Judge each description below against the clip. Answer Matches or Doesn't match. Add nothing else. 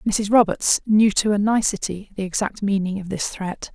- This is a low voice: Doesn't match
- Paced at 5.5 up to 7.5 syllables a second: Doesn't match